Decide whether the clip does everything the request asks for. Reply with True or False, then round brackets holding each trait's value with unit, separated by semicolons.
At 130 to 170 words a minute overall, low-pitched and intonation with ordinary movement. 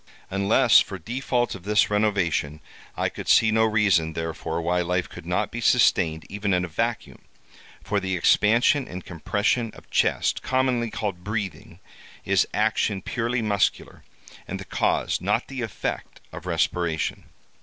True (150 wpm; 100 Hz; 4.0 semitones)